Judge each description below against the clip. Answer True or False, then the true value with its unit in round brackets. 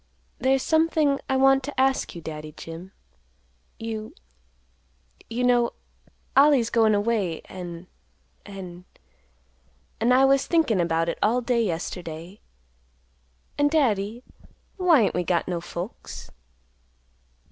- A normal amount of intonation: False (7.0 semitones)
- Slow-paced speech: True (105 wpm)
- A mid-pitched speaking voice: False (225 Hz)